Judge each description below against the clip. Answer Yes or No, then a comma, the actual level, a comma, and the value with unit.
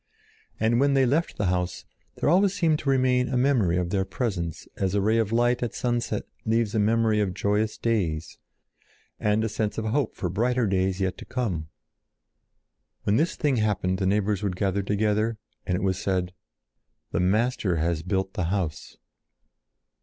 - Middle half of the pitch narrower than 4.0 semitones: No, average, 4.3 semitones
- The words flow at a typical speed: Yes, average, 175 wpm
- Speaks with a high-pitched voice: No, low, 105 Hz